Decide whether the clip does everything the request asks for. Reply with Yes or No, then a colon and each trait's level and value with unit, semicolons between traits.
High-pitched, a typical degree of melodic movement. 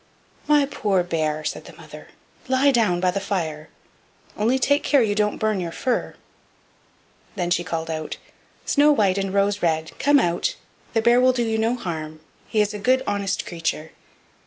No: high, 205 Hz; wide, 6.0 semitones